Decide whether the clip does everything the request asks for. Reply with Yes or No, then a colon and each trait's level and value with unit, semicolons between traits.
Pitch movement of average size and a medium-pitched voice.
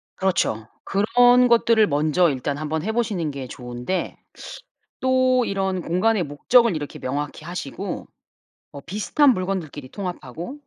No: wide, 7.5 semitones; medium, 180 Hz